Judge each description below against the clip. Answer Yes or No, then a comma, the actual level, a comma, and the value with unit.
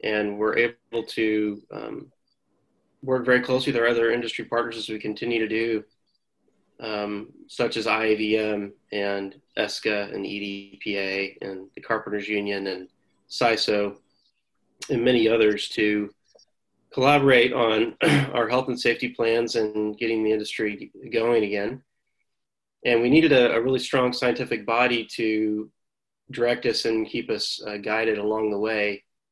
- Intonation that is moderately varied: No, narrow, 2.2 semitones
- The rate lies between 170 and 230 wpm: No, average, 140 wpm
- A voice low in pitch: Yes, low, 110 Hz